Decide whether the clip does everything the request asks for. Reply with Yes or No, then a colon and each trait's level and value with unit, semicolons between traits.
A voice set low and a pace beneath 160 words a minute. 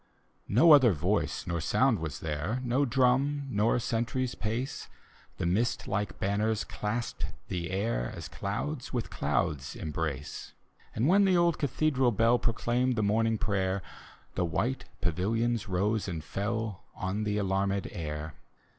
Yes: low, 110 Hz; average, 140 wpm